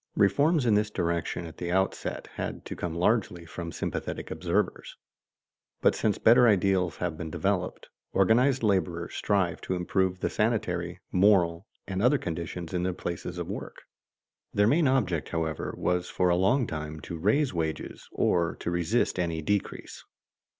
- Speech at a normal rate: Yes, average, 155 wpm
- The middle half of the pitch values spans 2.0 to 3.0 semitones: No, average, 3.7 semitones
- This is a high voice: No, very low, 90 Hz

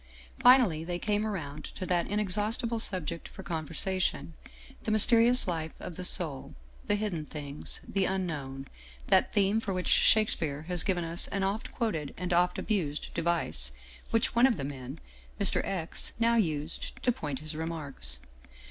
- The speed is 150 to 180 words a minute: Yes, average, 160 wpm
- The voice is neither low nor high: Yes, medium, 180 Hz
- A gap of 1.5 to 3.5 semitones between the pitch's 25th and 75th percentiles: No, average, 5.1 semitones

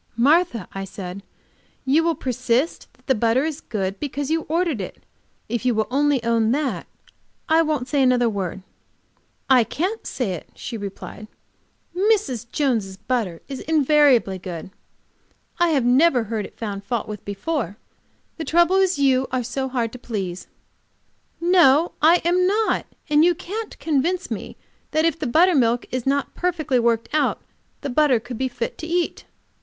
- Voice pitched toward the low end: No, very high, 265 Hz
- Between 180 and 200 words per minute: No, average, 160 wpm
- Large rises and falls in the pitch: Yes, wide, 5.8 semitones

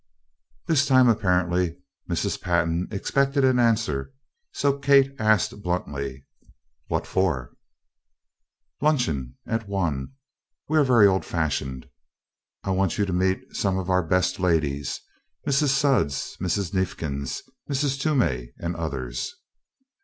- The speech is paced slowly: Yes, slow, 120 wpm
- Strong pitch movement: Yes, wide, 8.0 semitones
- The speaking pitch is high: No, very low, 95 Hz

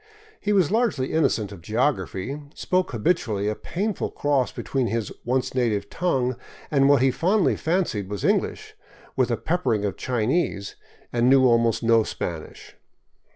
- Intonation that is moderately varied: No, wide, 6.9 semitones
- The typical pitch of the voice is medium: No, low, 125 Hz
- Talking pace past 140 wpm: Yes, average, 150 wpm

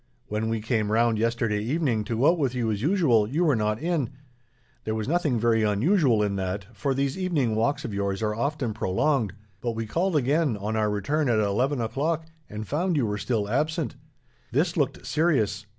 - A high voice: No, low, 115 Hz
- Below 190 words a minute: No, average, 200 wpm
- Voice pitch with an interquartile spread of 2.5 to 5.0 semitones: No, wide, 5.5 semitones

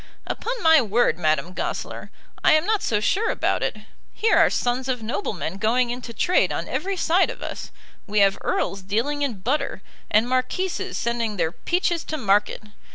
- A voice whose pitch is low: No, high, 245 Hz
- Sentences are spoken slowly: No, average, 175 wpm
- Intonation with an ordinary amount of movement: No, wide, 7.4 semitones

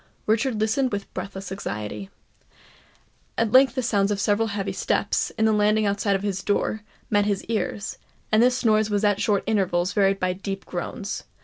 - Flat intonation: Yes, narrow, 1.9 semitones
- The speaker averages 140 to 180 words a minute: Yes, average, 175 wpm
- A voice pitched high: Yes, high, 205 Hz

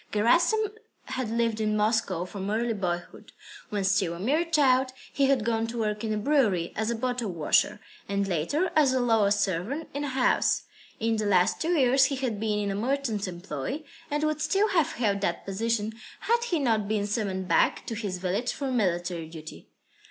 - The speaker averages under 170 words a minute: No, average, 190 wpm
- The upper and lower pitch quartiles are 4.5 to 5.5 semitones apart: Yes, average, 5.0 semitones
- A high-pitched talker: Yes, high, 220 Hz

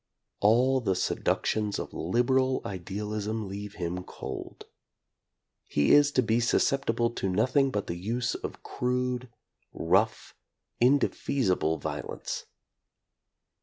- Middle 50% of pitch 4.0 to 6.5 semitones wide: Yes, average, 4.6 semitones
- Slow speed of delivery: Yes, slow, 110 wpm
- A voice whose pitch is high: No, low, 110 Hz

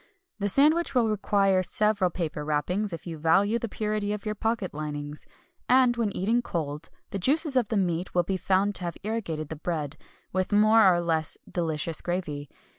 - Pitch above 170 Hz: Yes, high, 190 Hz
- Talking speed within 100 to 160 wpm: No, average, 185 wpm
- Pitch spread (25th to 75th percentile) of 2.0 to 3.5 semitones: No, average, 4.7 semitones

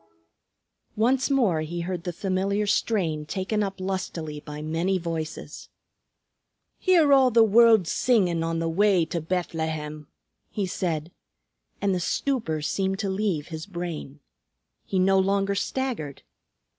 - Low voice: No, medium, 185 Hz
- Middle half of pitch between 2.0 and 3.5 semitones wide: No, average, 4.1 semitones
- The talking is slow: Yes, slow, 130 wpm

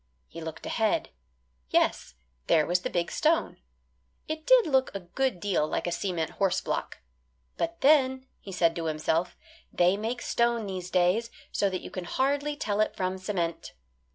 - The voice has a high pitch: Yes, high, 195 Hz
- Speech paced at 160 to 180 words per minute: Yes, average, 170 wpm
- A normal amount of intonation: No, wide, 6.9 semitones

